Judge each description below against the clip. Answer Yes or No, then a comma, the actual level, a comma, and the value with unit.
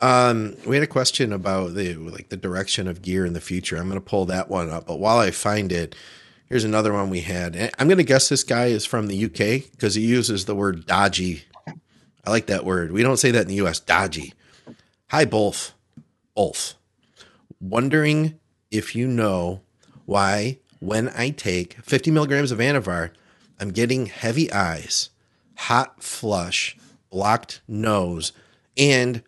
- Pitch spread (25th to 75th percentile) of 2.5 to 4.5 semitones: No, average, 5.2 semitones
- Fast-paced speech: No, average, 170 wpm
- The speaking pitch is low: Yes, low, 105 Hz